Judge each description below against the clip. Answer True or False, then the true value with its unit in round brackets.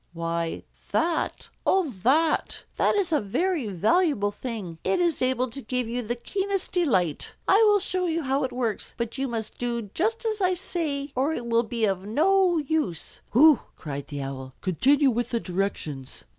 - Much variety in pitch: True (8.3 semitones)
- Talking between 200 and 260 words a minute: False (180 wpm)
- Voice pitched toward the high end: True (255 Hz)